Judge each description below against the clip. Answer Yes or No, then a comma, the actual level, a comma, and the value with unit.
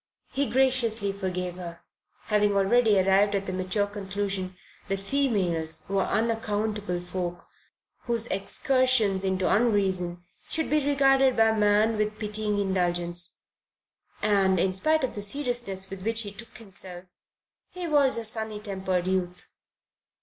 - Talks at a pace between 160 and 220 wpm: No, slow, 135 wpm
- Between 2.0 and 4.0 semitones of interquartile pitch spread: Yes, average, 3.3 semitones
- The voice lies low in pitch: No, high, 205 Hz